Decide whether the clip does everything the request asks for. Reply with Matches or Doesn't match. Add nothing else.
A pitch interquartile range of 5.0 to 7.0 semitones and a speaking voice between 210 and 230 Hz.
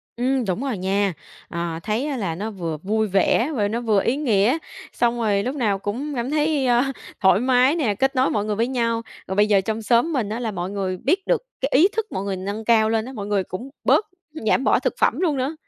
Doesn't match